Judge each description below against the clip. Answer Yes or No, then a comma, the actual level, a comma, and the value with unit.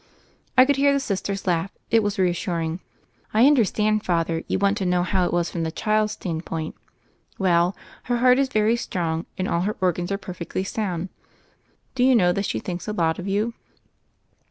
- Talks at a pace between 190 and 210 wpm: Yes, average, 195 wpm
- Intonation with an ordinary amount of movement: Yes, average, 3.7 semitones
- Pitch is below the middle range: No, high, 190 Hz